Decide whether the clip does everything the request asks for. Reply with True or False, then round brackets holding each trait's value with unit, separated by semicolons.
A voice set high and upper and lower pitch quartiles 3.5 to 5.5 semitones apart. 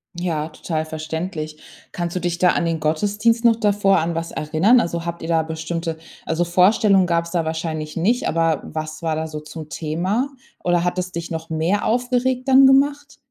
False (170 Hz; 4.1 semitones)